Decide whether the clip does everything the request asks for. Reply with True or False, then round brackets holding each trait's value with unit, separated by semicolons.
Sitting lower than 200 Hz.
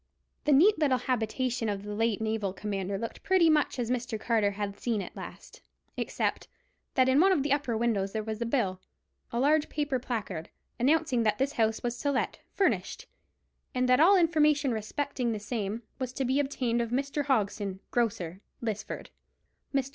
False (240 Hz)